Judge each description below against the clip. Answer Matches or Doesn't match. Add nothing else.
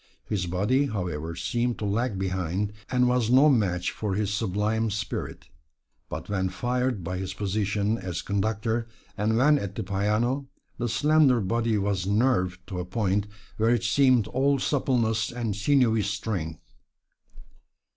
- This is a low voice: Matches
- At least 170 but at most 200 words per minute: Doesn't match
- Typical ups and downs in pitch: Matches